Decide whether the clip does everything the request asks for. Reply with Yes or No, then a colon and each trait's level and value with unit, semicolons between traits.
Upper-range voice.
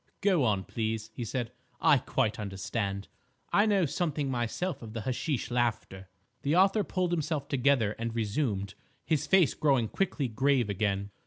No: low, 125 Hz